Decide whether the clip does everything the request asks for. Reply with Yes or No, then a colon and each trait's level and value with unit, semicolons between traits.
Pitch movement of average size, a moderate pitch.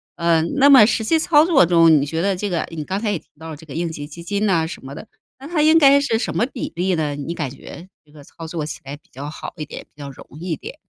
No: wide, 6.0 semitones; medium, 170 Hz